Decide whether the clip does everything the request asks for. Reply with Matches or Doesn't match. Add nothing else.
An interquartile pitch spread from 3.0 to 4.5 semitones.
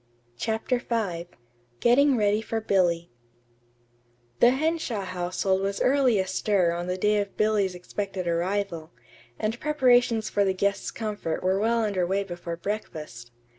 Matches